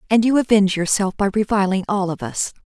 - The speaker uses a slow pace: No, average, 200 wpm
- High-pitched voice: Yes, high, 200 Hz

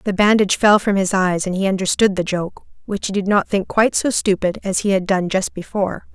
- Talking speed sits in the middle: No, fast, 245 wpm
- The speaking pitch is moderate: No, high, 195 Hz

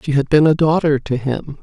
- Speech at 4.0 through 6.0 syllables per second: Yes, 5.3 syllables/s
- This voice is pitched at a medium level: Yes, medium, 145 Hz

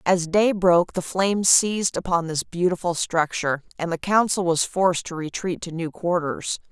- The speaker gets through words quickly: No, average, 180 wpm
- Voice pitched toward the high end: No, medium, 175 Hz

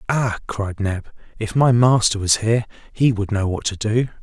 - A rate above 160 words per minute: Yes, average, 200 wpm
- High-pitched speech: No, low, 110 Hz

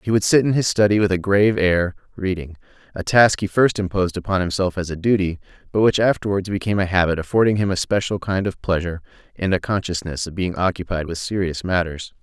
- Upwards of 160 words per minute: Yes, fast, 205 wpm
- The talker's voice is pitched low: Yes, very low, 95 Hz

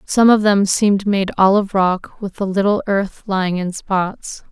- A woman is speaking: Yes, female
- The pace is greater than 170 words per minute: Yes, average, 200 wpm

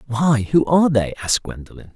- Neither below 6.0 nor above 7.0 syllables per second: Yes, 6.1 syllables/s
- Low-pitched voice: Yes, low, 130 Hz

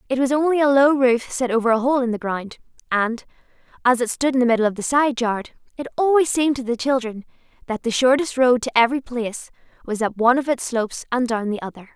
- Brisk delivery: Yes, fast, 235 wpm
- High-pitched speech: Yes, high, 245 Hz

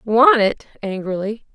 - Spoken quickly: No, slow, 115 wpm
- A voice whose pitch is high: Yes, high, 225 Hz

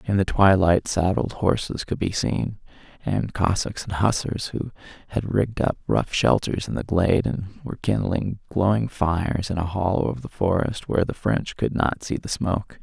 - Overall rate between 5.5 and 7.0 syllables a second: No, 4.9 syllables/s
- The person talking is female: No, male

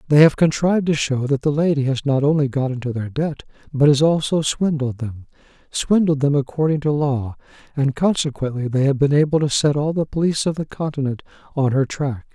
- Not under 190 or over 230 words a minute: Yes, average, 195 wpm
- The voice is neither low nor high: Yes, medium, 145 Hz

